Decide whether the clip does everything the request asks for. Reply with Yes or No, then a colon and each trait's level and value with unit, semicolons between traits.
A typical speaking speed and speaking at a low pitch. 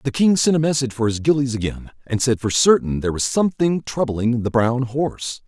No: fast, 220 wpm; low, 130 Hz